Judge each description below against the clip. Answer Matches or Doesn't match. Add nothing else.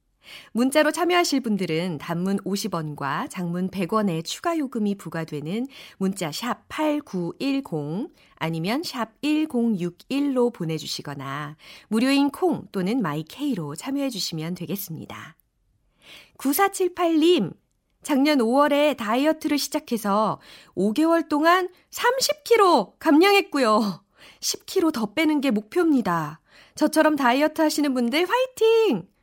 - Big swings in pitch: Matches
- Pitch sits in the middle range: Doesn't match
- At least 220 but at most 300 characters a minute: Matches